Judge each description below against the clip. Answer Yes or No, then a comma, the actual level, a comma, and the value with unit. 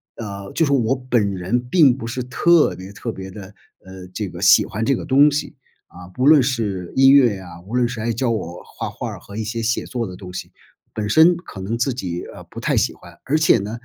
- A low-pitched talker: Yes, low, 115 Hz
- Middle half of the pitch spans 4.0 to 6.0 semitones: Yes, average, 5.1 semitones